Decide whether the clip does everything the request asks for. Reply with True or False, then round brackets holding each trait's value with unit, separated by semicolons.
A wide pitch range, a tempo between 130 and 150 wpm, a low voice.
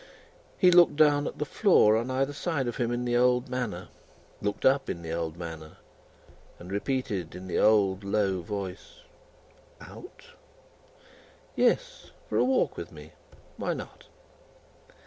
True (6.6 semitones; 145 wpm; 120 Hz)